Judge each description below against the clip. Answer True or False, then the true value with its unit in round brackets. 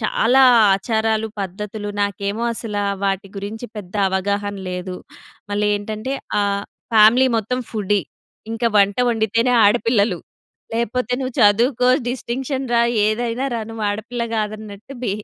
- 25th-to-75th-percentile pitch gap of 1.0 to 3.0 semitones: True (2.5 semitones)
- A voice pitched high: True (215 Hz)